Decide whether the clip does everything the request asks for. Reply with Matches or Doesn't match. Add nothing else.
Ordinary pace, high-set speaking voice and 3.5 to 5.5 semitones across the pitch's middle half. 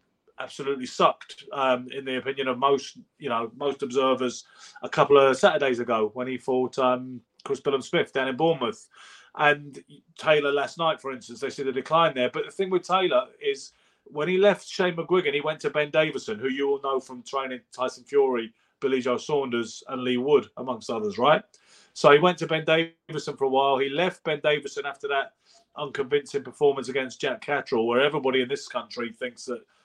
Doesn't match